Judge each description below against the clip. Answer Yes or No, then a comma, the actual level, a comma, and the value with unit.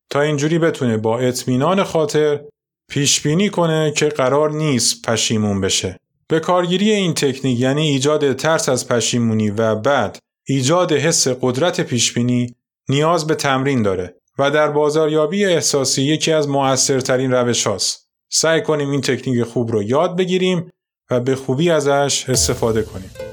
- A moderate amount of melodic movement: Yes, average, 3.9 semitones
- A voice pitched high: No, medium, 140 Hz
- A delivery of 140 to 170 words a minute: Yes, average, 145 wpm